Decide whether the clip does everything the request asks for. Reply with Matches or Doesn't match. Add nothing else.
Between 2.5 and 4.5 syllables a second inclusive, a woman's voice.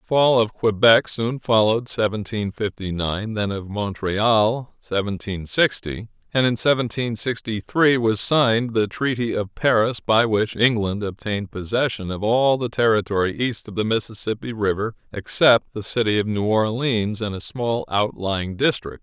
Doesn't match